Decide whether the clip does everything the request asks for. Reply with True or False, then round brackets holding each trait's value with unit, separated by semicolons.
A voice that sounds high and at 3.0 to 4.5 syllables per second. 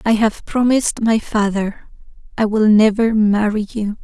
True (215 Hz; 4.4 syllables/s)